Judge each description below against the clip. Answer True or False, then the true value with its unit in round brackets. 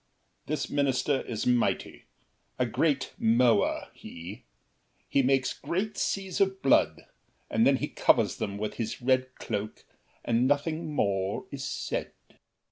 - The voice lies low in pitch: True (130 Hz)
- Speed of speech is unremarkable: False (130 wpm)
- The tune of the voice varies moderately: True (4.3 semitones)